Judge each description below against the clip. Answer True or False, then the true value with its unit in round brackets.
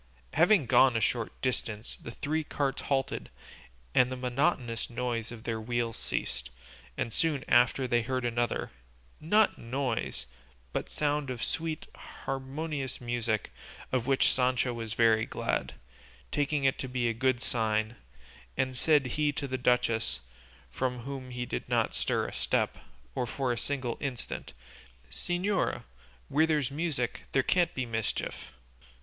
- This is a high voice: False (125 Hz)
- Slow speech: False (145 wpm)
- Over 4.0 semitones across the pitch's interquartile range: False (3.0 semitones)